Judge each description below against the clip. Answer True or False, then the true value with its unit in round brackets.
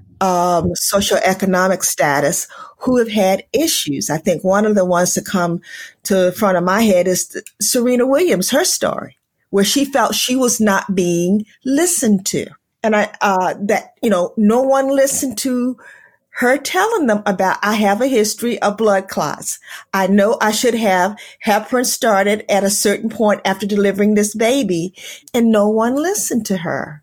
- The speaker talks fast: False (175 wpm)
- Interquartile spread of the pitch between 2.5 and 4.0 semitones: False (4.4 semitones)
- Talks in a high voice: True (205 Hz)